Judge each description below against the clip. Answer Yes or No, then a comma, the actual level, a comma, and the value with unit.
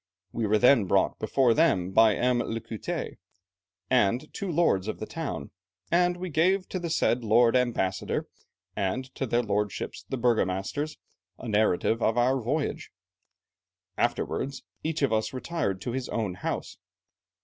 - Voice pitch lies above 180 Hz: No, low, 120 Hz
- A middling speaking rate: Yes, average, 150 wpm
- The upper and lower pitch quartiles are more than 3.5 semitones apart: Yes, average, 5.1 semitones